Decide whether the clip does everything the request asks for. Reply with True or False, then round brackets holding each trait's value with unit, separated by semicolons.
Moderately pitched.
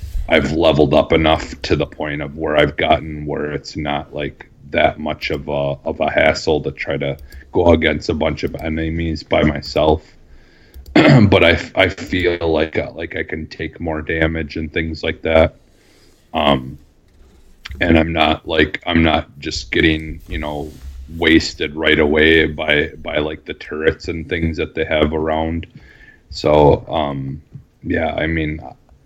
False (80 Hz)